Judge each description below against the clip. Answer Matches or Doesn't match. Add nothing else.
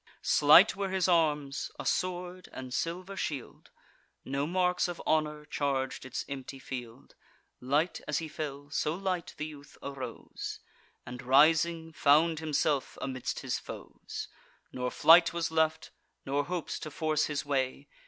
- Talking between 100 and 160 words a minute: Matches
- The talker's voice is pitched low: Doesn't match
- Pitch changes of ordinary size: Matches